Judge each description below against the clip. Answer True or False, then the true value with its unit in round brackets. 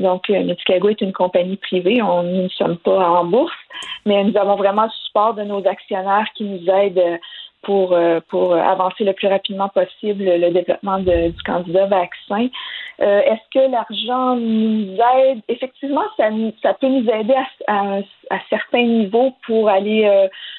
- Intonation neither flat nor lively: True (3.5 semitones)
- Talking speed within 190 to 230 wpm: False (170 wpm)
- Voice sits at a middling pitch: False (200 Hz)